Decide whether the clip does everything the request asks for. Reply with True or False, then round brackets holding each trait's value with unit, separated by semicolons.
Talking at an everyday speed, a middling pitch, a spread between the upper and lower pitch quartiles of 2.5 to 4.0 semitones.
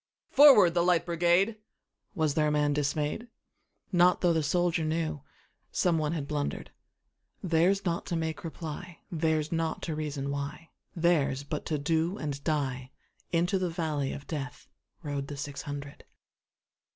False (125 wpm; 160 Hz; 3.0 semitones)